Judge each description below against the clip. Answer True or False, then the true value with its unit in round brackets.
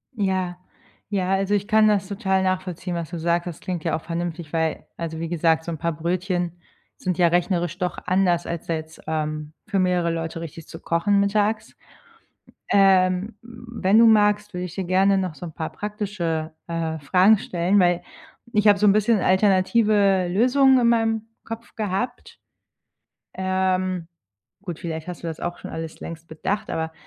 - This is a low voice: False (185 Hz)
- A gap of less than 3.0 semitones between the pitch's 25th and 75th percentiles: False (3.3 semitones)